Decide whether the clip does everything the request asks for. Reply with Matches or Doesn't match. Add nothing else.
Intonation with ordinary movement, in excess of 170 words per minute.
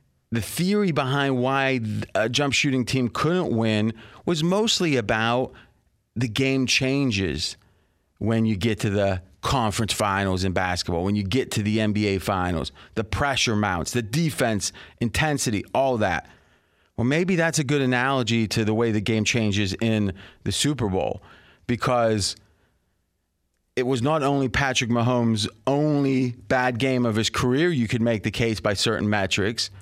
Doesn't match